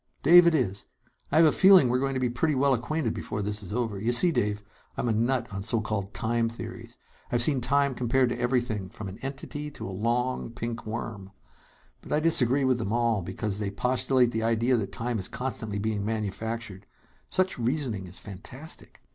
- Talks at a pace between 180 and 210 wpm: Yes, average, 200 wpm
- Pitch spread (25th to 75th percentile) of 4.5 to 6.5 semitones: No, average, 3.5 semitones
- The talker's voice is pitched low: Yes, low, 120 Hz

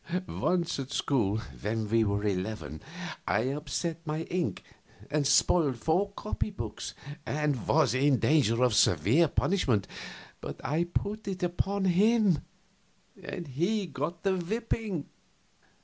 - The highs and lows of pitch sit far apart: Yes, wide, 6.7 semitones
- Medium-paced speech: No, slow, 130 wpm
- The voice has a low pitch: No, medium, 150 Hz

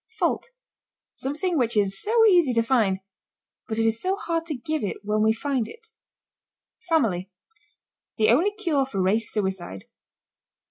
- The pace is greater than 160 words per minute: No, average, 150 wpm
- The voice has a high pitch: Yes, high, 240 Hz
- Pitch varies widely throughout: Yes, wide, 7.6 semitones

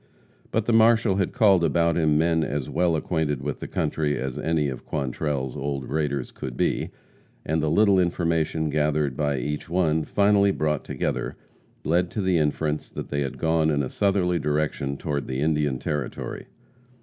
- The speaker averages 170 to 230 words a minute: Yes, average, 175 wpm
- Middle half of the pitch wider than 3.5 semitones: No, average, 3.0 semitones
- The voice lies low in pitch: Yes, very low, 75 Hz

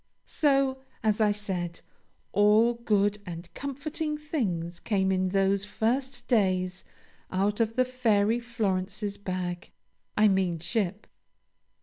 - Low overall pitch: No, high, 205 Hz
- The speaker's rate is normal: No, slow, 115 wpm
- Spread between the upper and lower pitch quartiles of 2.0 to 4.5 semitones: Yes, average, 4.1 semitones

